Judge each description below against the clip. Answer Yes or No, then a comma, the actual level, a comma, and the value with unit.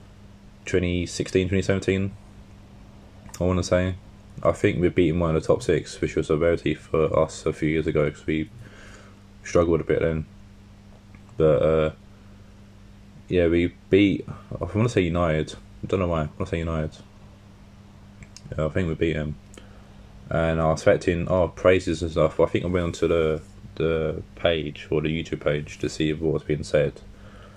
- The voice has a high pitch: No, very low, 95 Hz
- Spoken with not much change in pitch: No, average, 3.7 semitones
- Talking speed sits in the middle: Yes, average, 180 wpm